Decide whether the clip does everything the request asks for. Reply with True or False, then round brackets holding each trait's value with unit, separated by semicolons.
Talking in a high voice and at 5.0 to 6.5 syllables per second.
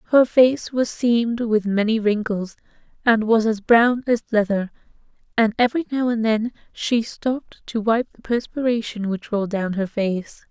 False (225 Hz; 4.7 syllables/s)